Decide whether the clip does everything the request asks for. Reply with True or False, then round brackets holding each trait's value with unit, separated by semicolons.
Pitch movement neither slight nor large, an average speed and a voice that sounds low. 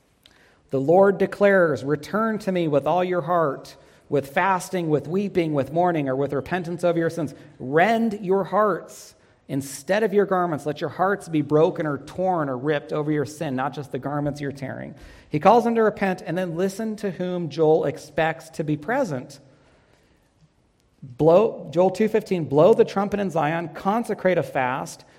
False (4.5 semitones; 175 wpm; 165 Hz)